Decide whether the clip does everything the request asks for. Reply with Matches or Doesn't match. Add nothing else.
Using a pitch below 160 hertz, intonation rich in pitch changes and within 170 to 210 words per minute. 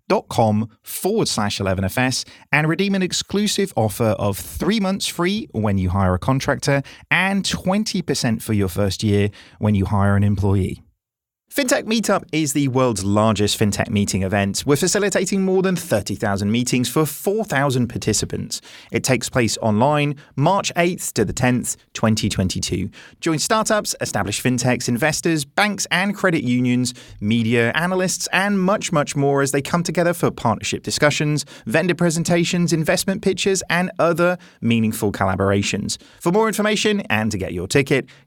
Doesn't match